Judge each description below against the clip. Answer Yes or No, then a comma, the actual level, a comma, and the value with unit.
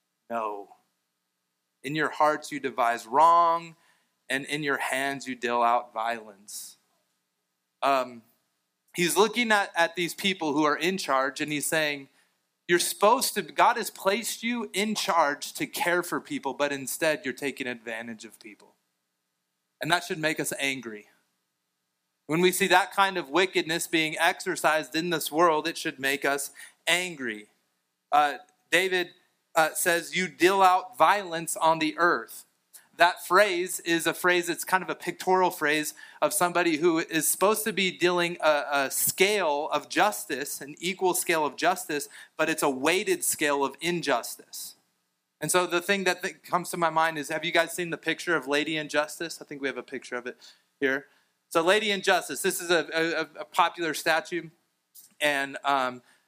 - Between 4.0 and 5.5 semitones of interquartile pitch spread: Yes, average, 5.2 semitones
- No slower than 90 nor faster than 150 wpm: No, average, 170 wpm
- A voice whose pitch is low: No, medium, 155 Hz